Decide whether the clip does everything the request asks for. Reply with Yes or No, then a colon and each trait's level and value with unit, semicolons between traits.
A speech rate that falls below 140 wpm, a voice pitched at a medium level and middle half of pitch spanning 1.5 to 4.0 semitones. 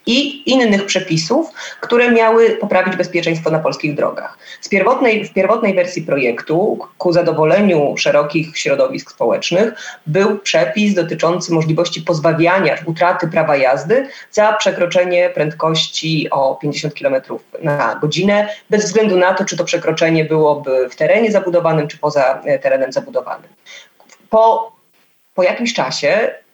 No: average, 125 wpm; medium, 180 Hz; average, 4.9 semitones